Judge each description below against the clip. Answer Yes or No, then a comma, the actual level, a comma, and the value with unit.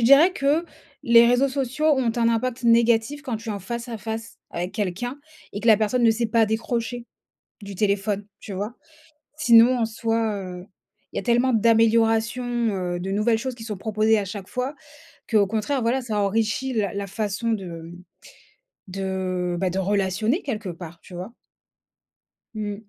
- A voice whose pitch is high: Yes, high, 225 Hz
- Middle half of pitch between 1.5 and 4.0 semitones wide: Yes, average, 3.1 semitones